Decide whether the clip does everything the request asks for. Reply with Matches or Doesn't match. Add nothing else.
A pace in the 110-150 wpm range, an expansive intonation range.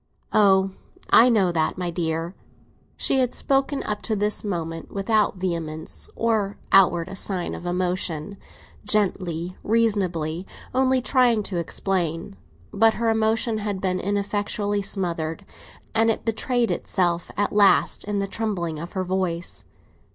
Doesn't match